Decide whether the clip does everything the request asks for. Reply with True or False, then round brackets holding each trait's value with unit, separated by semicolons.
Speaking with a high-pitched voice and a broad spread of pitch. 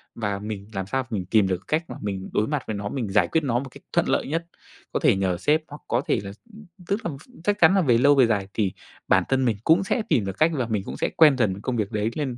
False (115 Hz; 6.6 semitones)